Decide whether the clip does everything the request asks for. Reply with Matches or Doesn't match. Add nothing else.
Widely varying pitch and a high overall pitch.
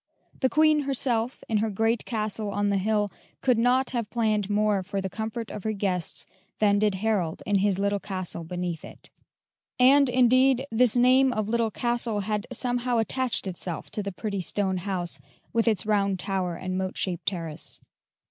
Doesn't match